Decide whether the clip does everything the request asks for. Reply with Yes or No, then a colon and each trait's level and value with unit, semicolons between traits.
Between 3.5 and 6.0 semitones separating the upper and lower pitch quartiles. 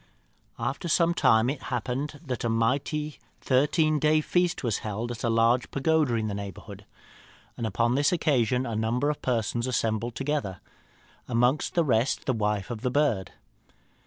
Yes: average, 4.4 semitones